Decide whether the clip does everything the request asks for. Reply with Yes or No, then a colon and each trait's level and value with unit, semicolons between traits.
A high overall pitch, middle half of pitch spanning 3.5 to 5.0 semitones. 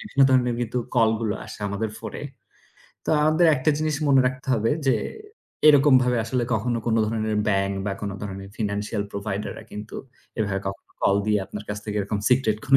No: low, 110 Hz; average, 3.8 semitones